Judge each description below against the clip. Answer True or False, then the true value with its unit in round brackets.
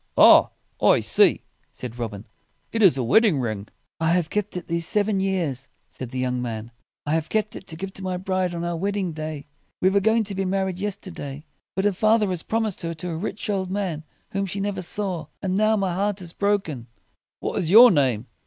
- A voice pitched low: False (185 Hz)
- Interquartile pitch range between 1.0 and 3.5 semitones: False (4.5 semitones)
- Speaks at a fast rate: True (225 wpm)